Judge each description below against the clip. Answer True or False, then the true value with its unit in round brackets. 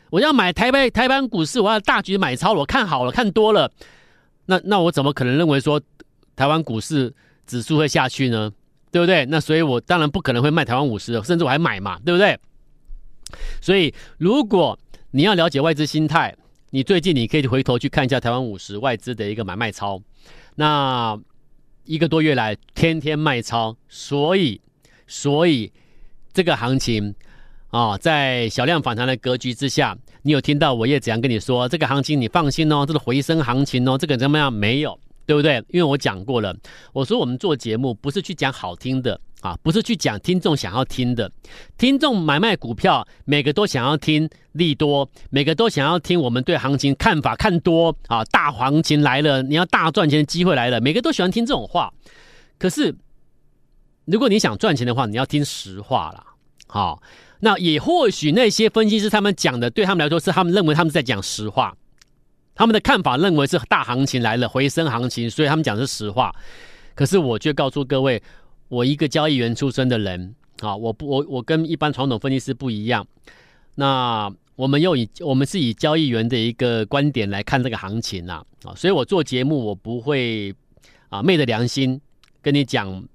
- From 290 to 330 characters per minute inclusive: True (295 characters per minute)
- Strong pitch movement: False (4.7 semitones)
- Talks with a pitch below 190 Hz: True (140 Hz)